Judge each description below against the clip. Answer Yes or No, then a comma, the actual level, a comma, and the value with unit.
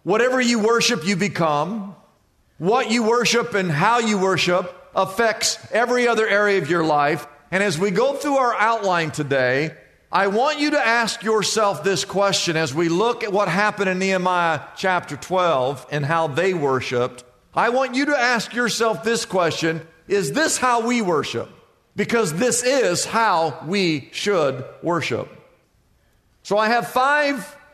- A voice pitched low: No, high, 200 Hz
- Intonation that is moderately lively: No, wide, 6.1 semitones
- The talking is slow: No, average, 160 wpm